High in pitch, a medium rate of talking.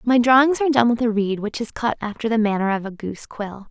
No: high, 220 Hz; fast, 275 wpm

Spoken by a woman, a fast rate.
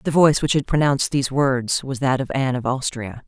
Yes: female; fast, 240 wpm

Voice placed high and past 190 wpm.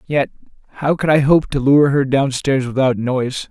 No: low, 135 Hz; fast, 205 wpm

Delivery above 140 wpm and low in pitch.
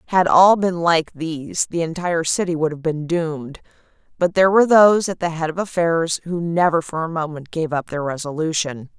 No: average, 200 wpm; medium, 165 Hz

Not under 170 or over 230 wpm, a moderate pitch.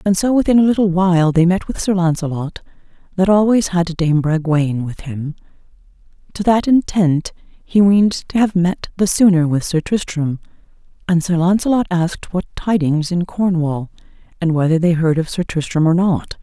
Yes: average, 175 wpm; medium, 175 Hz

